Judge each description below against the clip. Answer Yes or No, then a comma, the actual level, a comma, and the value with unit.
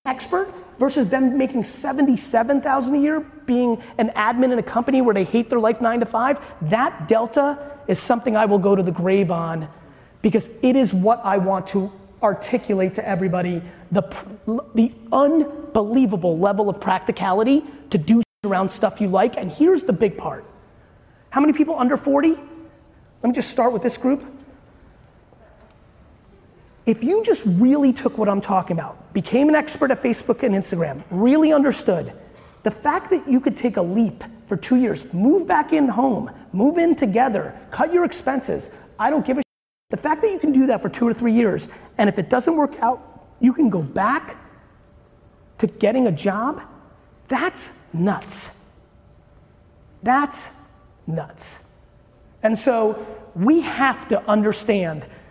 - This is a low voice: No, high, 235 Hz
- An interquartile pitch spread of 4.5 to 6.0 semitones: Yes, average, 5.1 semitones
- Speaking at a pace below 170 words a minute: Yes, average, 160 wpm